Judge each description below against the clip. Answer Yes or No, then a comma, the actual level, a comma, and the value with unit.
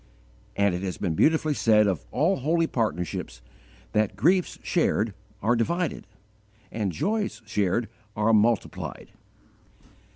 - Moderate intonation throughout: No, wide, 7.9 semitones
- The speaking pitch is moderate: No, low, 110 Hz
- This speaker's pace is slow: Yes, slow, 120 wpm